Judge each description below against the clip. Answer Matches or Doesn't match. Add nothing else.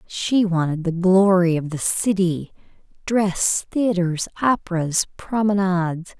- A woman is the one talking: Matches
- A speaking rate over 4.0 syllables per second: Doesn't match